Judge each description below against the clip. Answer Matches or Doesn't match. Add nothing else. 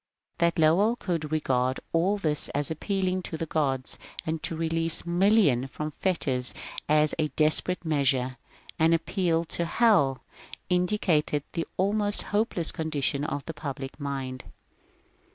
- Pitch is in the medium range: Matches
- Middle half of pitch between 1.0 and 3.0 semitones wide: Doesn't match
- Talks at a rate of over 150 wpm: Doesn't match